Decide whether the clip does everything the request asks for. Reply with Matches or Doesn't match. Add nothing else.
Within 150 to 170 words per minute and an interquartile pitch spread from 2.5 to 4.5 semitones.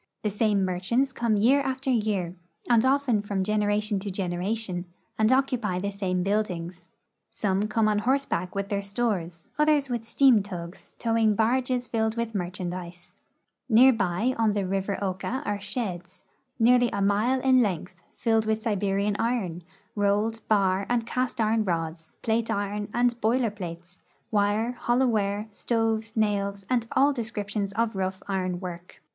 Matches